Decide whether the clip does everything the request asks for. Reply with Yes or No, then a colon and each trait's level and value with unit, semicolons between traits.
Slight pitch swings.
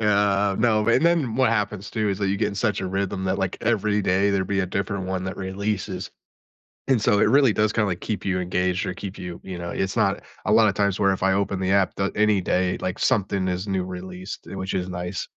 Yes: narrow, 2.1 semitones